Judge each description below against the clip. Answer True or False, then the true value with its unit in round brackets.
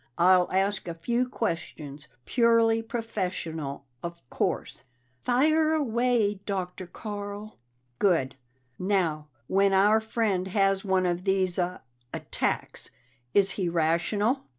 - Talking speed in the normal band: False (110 wpm)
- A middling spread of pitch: True (4.1 semitones)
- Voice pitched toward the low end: False (195 Hz)